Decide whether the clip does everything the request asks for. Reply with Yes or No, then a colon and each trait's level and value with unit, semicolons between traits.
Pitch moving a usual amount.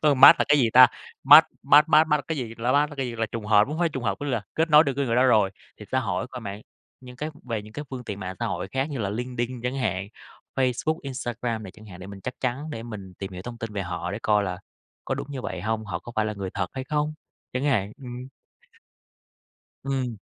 Yes: average, 4.6 semitones